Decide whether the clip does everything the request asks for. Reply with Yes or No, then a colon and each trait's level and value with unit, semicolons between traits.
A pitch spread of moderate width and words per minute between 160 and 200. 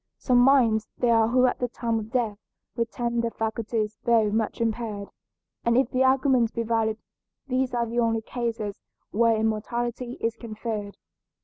No: narrow, 1.6 semitones; average, 165 wpm